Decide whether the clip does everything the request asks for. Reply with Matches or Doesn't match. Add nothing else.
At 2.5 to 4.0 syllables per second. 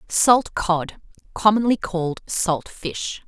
Matches